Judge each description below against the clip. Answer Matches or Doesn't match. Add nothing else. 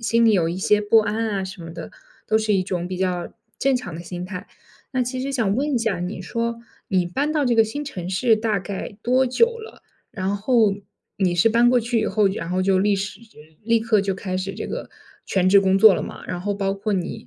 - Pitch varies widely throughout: Doesn't match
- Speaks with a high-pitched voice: Matches